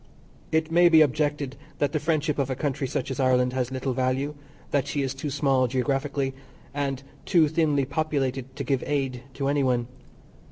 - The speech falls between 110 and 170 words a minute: No, average, 185 wpm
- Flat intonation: Yes, narrow, 2.1 semitones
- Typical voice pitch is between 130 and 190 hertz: Yes, medium, 140 Hz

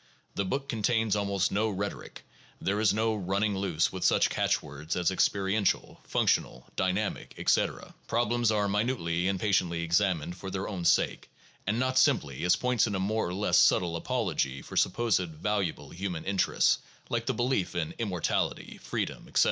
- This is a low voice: Yes, low, 100 Hz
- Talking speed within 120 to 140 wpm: No, average, 165 wpm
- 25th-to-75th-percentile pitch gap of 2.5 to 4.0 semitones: Yes, average, 3.5 semitones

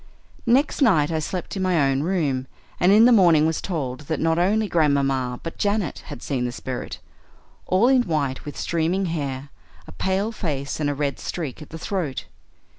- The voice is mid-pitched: Yes, medium, 160 Hz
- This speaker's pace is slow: No, average, 190 wpm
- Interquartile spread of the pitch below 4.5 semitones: No, wide, 5.4 semitones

